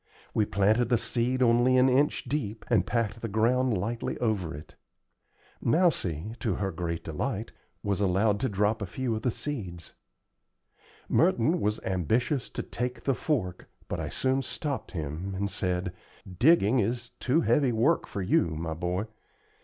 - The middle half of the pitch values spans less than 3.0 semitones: No, average, 5.2 semitones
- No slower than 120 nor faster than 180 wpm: Yes, average, 160 wpm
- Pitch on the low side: Yes, low, 110 Hz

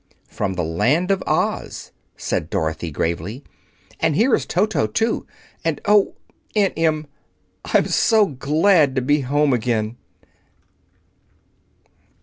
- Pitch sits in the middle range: Yes, medium, 145 Hz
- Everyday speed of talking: No, slow, 125 wpm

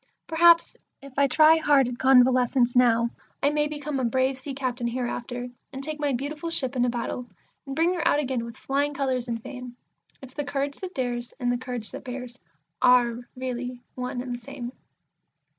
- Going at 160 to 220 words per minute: Yes, average, 190 wpm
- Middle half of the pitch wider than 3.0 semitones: No, narrow, 2.5 semitones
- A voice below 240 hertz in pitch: No, very high, 255 Hz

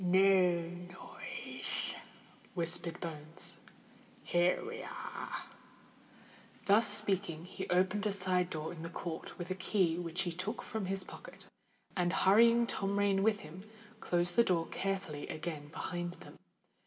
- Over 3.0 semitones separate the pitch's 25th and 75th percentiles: No, narrow, 2.4 semitones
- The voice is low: No, medium, 180 Hz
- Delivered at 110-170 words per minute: Yes, average, 140 wpm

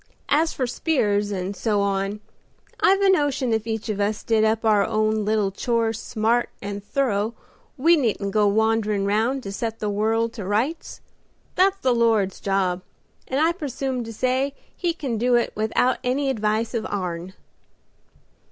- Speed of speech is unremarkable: Yes, average, 165 wpm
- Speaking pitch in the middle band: No, high, 225 Hz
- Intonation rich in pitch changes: No, average, 3.8 semitones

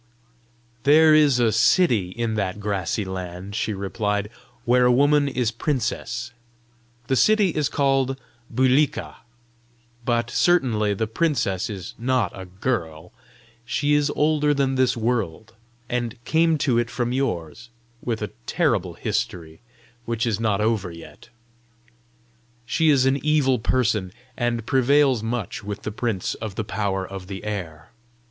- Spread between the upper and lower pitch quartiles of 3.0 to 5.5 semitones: Yes, average, 4.6 semitones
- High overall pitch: No, low, 115 Hz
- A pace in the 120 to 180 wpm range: Yes, average, 140 wpm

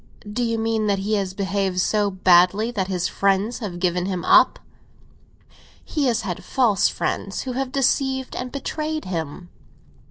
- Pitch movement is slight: No, average, 4.6 semitones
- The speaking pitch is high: Yes, high, 205 Hz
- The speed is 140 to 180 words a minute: Yes, average, 160 wpm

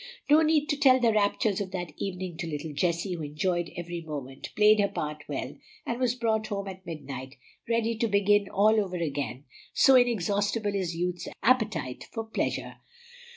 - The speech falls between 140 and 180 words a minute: Yes, average, 175 wpm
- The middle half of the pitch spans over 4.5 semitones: Yes, average, 5.0 semitones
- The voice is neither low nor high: No, high, 195 Hz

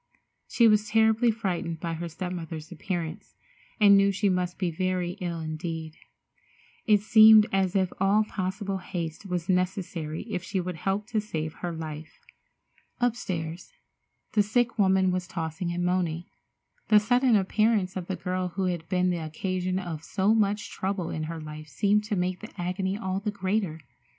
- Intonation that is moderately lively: Yes, average, 3.2 semitones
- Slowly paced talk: No, average, 170 wpm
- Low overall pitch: No, medium, 185 Hz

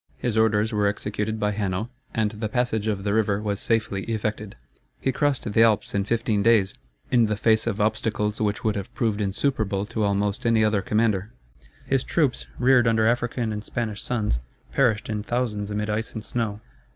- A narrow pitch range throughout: Yes, narrow, 1.8 semitones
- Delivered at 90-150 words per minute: No, average, 185 wpm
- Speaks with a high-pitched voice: No, low, 110 Hz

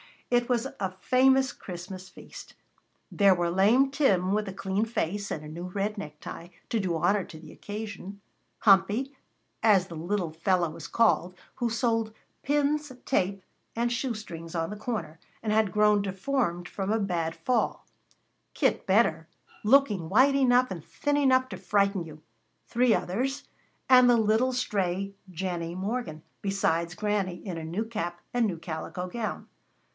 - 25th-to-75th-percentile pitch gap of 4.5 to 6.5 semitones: Yes, average, 5.0 semitones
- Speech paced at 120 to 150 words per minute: No, average, 160 wpm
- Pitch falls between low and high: No, high, 200 Hz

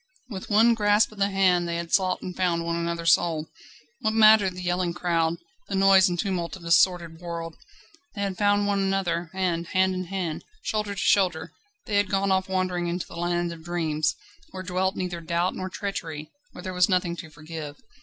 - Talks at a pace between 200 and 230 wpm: Yes, fast, 205 wpm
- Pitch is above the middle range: No, medium, 180 Hz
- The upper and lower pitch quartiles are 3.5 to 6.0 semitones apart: No, narrow, 2.4 semitones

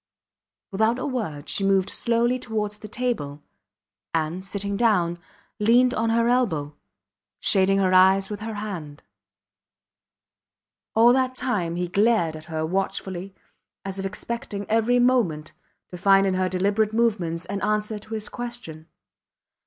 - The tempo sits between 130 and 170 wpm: Yes, average, 140 wpm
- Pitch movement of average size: Yes, average, 4.0 semitones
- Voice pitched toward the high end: Yes, high, 200 Hz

